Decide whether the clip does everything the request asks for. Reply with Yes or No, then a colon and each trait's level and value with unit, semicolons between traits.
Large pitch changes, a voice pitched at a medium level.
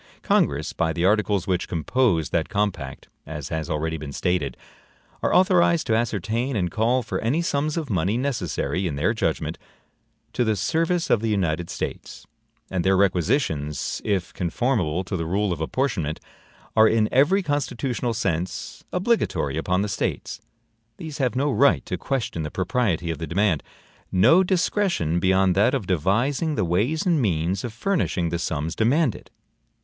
No: wide, 7.6 semitones; low, 100 Hz